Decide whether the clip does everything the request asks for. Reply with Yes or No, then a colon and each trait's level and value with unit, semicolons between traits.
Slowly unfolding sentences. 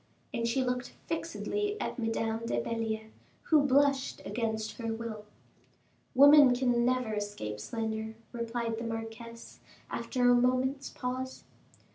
Yes: slow, 125 wpm